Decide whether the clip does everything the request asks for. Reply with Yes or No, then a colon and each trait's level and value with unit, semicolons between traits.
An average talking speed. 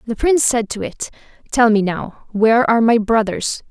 Yes: average, 195 wpm